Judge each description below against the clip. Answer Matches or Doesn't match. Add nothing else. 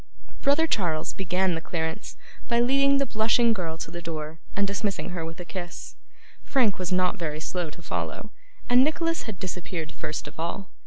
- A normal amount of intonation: Doesn't match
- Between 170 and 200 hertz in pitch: Matches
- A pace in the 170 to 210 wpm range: Matches